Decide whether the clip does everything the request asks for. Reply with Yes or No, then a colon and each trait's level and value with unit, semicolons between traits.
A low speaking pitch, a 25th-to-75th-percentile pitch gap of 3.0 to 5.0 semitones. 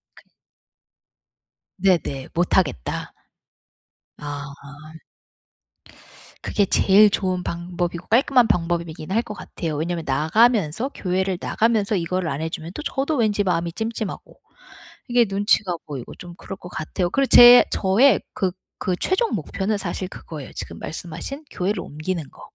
No: medium, 185 Hz; average, 4.5 semitones